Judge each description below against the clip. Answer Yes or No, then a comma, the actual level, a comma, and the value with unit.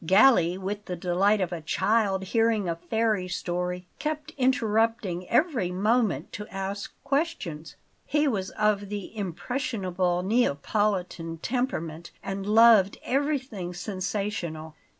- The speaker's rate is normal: No, slow, 115 wpm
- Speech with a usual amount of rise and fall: Yes, average, 4.2 semitones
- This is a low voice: No, high, 200 Hz